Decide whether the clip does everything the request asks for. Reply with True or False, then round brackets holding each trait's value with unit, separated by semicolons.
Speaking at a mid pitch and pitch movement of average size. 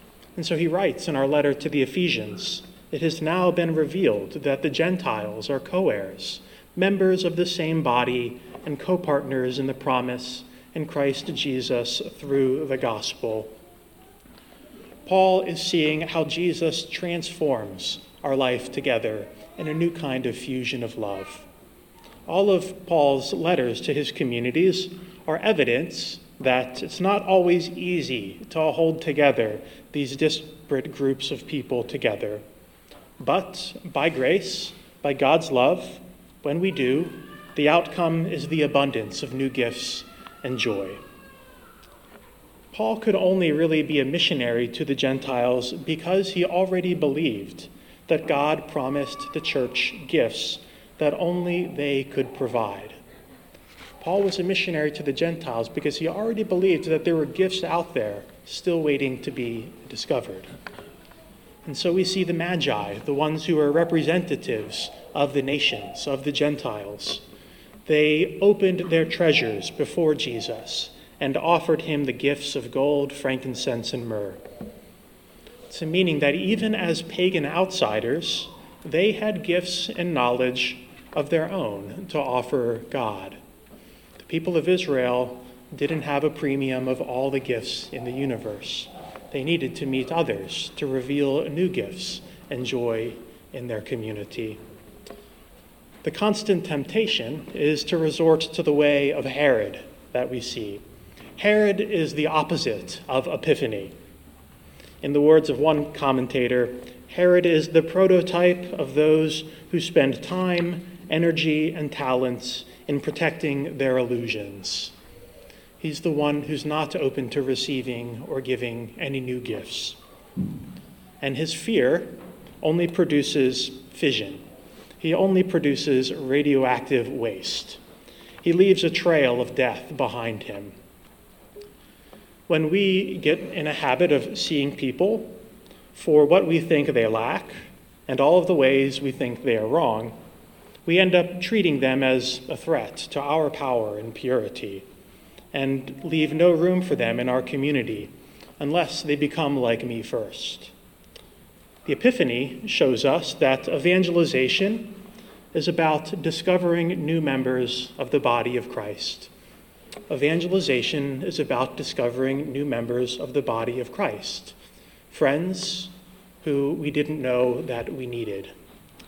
True (150 Hz; 5.0 semitones)